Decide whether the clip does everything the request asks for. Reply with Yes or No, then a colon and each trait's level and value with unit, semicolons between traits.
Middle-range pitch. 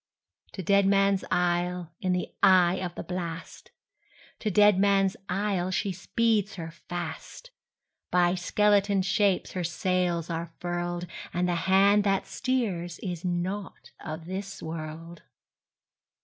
Yes: medium, 180 Hz